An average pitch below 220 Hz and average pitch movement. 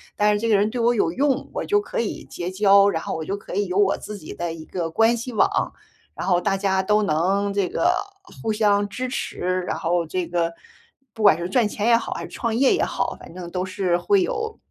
Yes: high, 200 Hz; average, 4.3 semitones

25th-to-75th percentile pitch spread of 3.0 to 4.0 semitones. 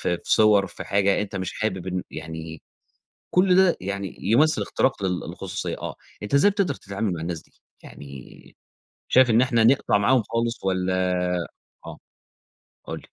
No: average, 4.6 semitones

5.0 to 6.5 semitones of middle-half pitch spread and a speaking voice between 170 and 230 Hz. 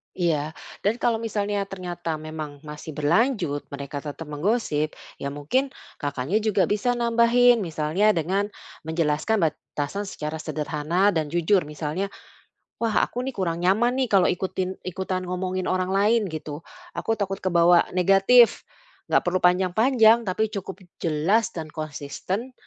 Yes: average, 5.3 semitones; medium, 185 Hz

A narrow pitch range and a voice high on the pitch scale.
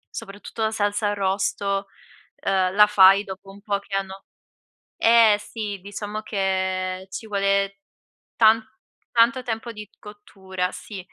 Yes: narrow, 1.6 semitones; high, 200 Hz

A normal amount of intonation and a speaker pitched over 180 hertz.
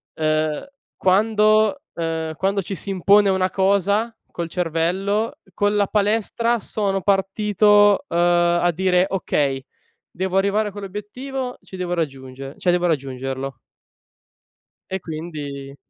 Yes: average, 4.1 semitones; high, 190 Hz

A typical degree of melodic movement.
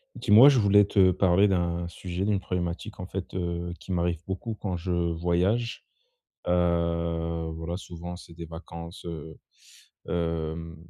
No: narrow, 2.0 semitones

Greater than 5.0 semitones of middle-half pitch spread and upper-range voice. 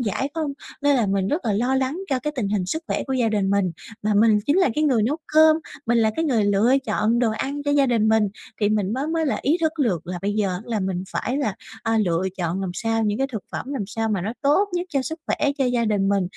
Yes: wide, 5.5 semitones; high, 225 Hz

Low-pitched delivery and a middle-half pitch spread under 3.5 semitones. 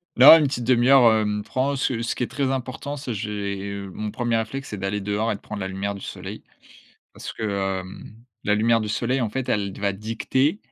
No: low, 110 Hz; average, 3.8 semitones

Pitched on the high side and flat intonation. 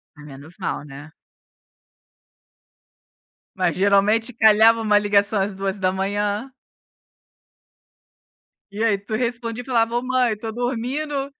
No: high, 215 Hz; average, 3.2 semitones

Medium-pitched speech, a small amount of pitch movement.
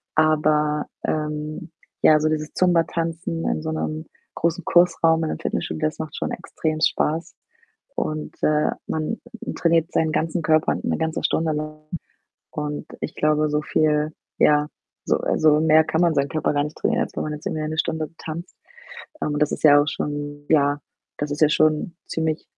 Yes: medium, 155 Hz; narrow, 1.1 semitones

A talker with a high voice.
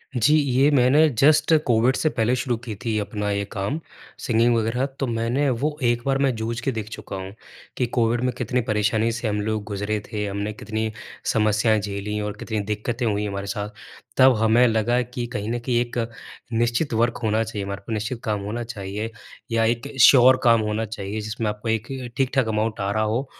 No: low, 115 Hz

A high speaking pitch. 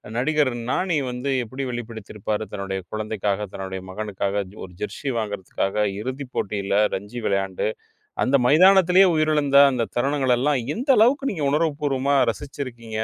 No: low, 125 Hz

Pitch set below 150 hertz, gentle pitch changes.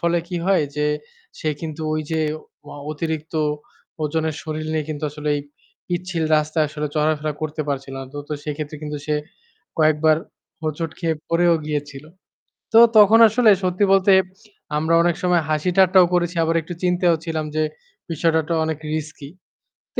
No: medium, 160 Hz; narrow, 2.3 semitones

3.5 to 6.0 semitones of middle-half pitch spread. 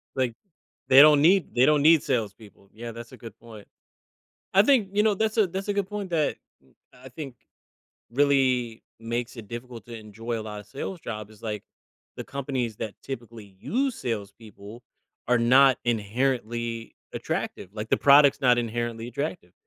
Yes: average, 4.1 semitones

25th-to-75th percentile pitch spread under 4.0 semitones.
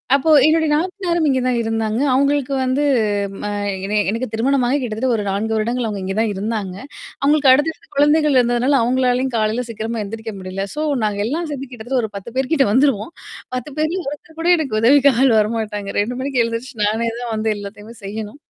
No: average, 4.3 semitones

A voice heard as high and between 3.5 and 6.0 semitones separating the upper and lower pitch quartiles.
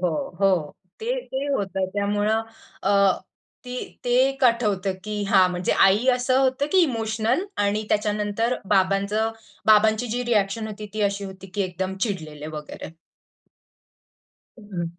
No: high, 210 Hz; average, 2.9 semitones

